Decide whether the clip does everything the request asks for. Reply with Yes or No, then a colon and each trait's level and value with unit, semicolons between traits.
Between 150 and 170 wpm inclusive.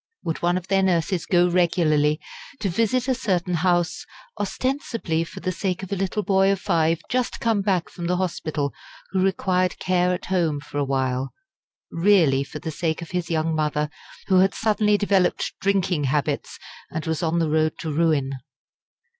No: average, 180 wpm